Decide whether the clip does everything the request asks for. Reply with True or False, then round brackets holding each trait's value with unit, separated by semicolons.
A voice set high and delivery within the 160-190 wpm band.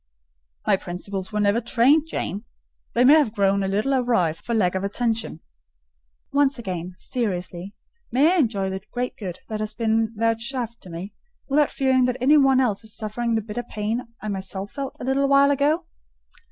True (225 Hz; 180 wpm)